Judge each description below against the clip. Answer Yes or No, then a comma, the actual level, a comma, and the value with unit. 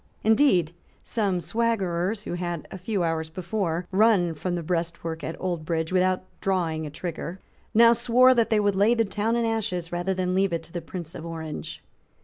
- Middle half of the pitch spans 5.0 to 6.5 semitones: No, average, 4.2 semitones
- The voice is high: No, medium, 180 Hz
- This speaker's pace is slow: No, average, 185 wpm